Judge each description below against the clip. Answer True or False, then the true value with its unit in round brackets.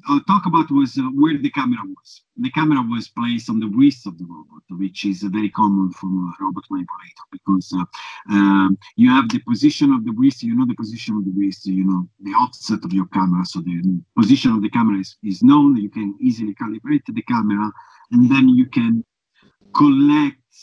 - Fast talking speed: True (210 wpm)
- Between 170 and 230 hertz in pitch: False (140 Hz)